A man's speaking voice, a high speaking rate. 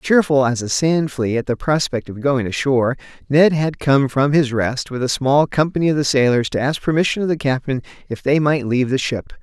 Yes: male; fast, 230 wpm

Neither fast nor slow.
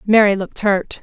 Yes: average, 175 wpm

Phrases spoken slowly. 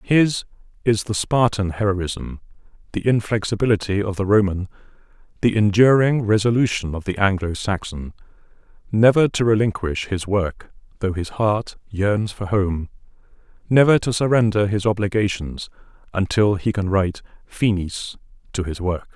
Yes: slow, 125 wpm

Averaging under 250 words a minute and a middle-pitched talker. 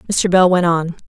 Yes: fast, 220 wpm; medium, 175 Hz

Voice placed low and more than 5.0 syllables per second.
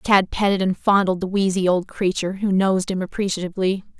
No: high, 190 Hz; 6.0 syllables/s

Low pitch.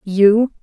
No: high, 210 Hz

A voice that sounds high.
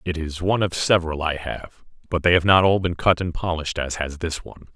No: very low, 85 Hz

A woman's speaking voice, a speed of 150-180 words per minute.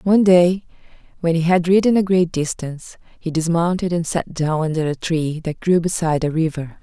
No: female; average, 195 wpm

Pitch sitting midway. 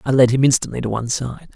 No: low, 125 Hz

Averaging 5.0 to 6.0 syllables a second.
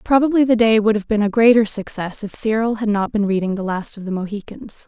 Yes: 5.9 syllables/s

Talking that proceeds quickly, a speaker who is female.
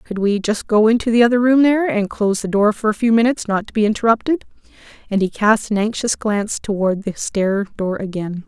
Yes: fast, 225 wpm; female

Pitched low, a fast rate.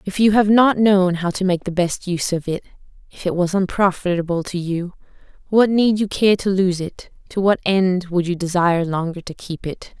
No: medium, 185 Hz; fast, 215 wpm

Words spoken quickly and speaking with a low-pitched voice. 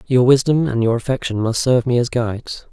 Yes: fast, 220 wpm; low, 125 Hz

